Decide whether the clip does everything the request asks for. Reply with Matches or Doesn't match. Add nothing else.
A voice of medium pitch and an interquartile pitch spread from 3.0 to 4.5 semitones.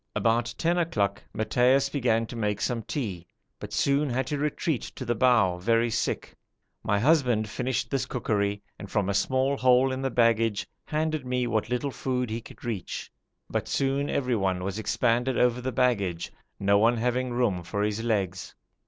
Doesn't match